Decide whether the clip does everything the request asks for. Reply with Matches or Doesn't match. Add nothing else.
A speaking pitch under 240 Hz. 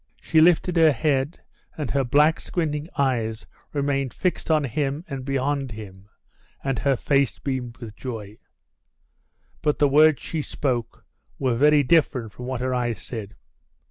Matches